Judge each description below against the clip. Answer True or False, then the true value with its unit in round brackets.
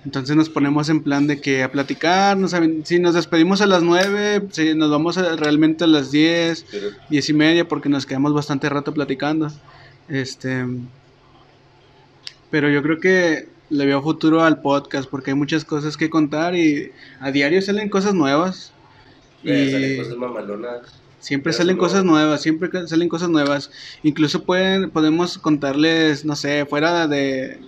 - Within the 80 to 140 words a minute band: False (165 wpm)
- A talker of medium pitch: True (150 Hz)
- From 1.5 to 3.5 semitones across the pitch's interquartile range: True (3.1 semitones)